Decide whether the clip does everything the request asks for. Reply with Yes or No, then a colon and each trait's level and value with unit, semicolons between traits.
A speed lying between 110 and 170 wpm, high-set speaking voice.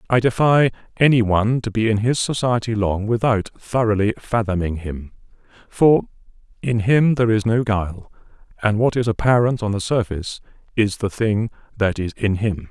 No: average, 165 wpm; low, 110 Hz